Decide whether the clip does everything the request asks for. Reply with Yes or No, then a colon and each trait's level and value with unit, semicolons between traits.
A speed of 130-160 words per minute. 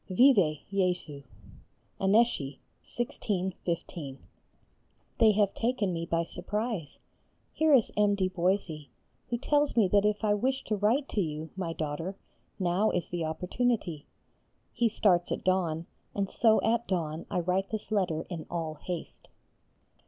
Yes: average, 145 wpm